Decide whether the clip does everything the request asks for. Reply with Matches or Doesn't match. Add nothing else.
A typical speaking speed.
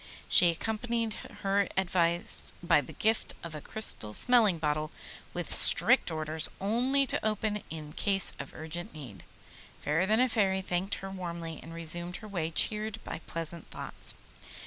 Matches